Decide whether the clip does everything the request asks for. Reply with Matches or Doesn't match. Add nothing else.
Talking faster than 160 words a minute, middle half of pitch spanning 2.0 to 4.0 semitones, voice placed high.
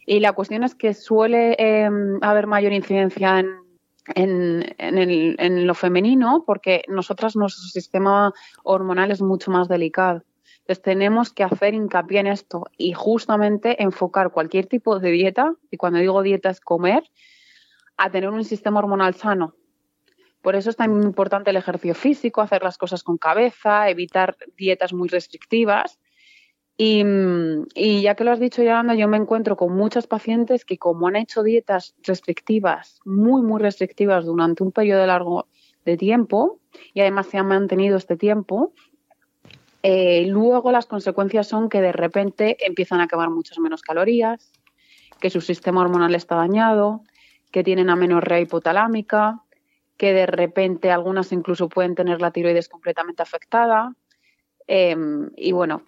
Doesn't match